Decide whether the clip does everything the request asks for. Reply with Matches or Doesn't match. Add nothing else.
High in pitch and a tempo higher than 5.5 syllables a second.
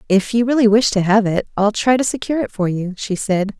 Matches